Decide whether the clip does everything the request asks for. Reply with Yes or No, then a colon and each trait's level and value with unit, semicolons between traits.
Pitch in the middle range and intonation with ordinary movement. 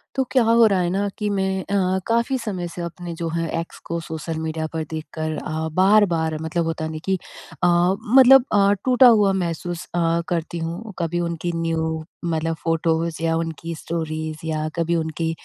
Yes: medium, 170 Hz; average, 3.0 semitones